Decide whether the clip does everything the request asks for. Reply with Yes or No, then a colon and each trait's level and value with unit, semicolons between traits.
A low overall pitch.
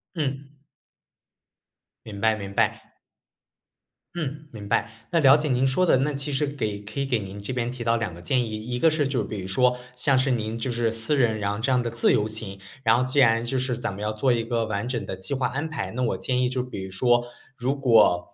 Yes: low, 120 Hz